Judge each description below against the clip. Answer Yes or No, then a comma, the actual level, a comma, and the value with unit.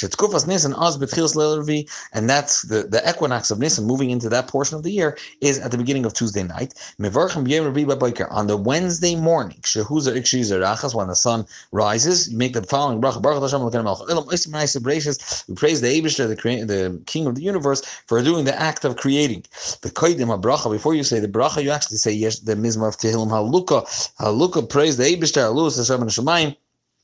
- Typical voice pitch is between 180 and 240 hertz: No, low, 135 Hz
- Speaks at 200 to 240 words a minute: No, average, 155 wpm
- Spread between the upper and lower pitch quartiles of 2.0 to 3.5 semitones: No, average, 5.2 semitones